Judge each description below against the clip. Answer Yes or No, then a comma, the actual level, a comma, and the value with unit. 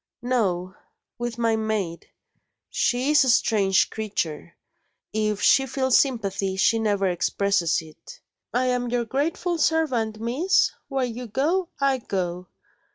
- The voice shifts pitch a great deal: No, average, 5.0 semitones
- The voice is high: Yes, high, 230 Hz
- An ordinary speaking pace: No, slow, 130 wpm